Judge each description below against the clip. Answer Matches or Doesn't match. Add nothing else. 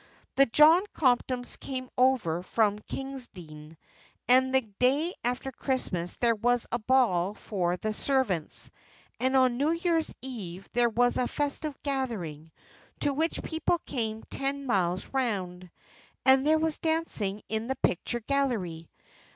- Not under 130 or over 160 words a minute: Matches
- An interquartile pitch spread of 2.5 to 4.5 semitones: Doesn't match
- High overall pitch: Matches